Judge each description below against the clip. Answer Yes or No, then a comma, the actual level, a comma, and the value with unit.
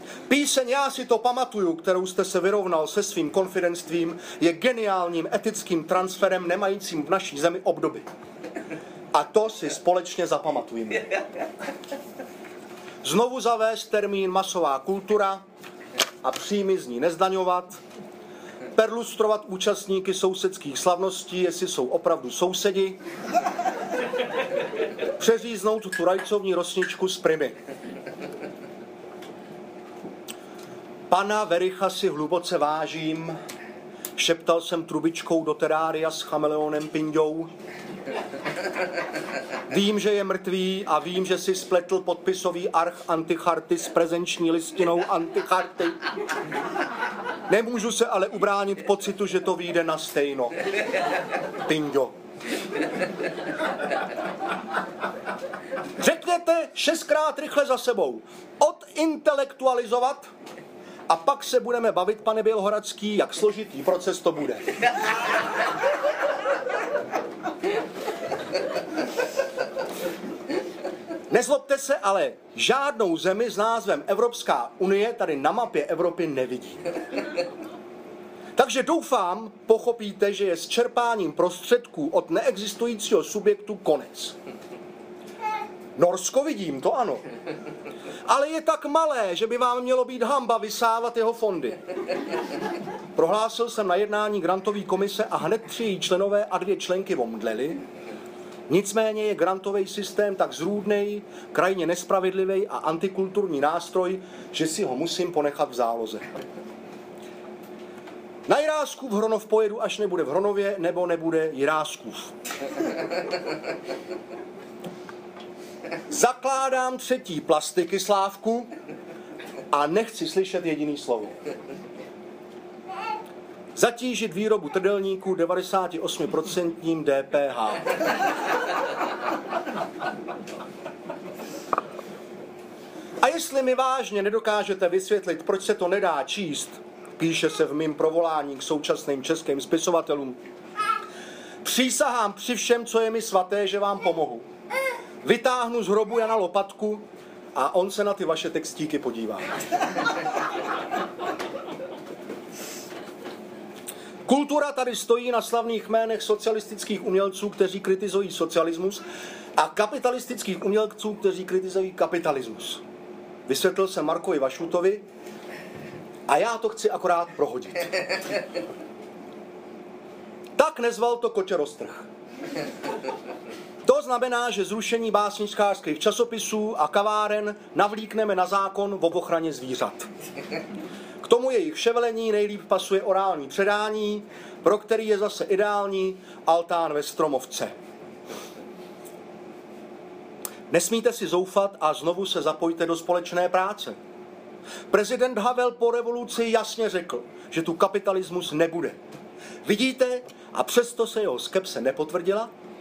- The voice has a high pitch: Yes, high, 195 Hz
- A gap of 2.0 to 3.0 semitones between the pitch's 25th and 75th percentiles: No, average, 4.7 semitones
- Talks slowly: Yes, slow, 100 wpm